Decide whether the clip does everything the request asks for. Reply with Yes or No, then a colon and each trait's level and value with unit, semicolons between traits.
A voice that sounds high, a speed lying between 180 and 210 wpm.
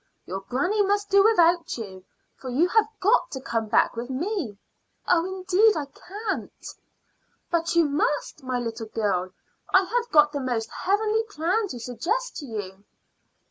No: very high, 330 Hz; average, 160 wpm